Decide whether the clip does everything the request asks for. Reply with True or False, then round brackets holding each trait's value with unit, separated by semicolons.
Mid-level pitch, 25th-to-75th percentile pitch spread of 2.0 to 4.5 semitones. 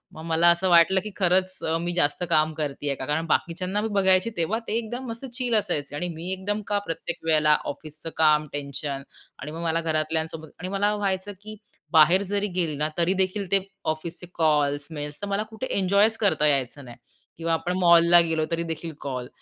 True (170 Hz; 3.8 semitones)